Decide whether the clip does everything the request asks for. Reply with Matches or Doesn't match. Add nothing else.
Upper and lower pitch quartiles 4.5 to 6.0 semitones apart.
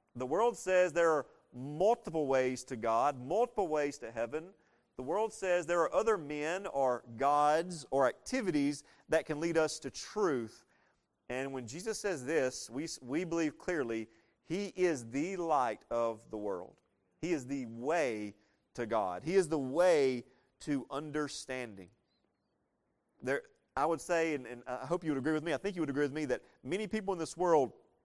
Matches